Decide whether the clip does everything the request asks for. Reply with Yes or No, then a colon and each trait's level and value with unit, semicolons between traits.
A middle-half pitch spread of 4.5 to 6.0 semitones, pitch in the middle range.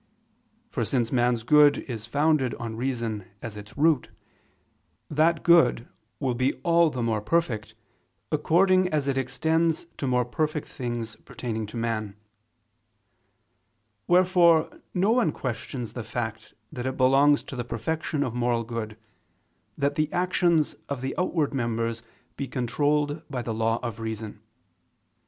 No: average, 4.9 semitones; low, 130 Hz